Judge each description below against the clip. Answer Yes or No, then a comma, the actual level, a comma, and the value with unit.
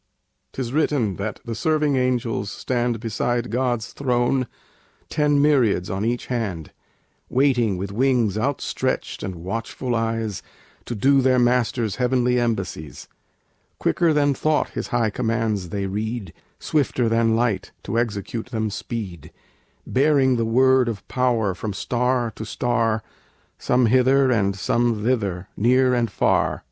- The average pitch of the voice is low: Yes, low, 120 Hz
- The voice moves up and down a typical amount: Yes, average, 3.0 semitones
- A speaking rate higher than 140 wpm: No, slow, 135 wpm